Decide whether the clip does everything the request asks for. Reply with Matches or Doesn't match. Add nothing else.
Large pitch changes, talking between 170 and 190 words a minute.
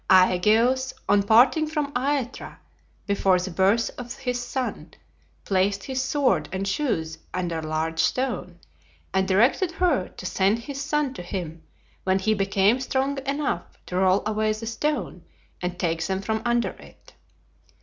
Doesn't match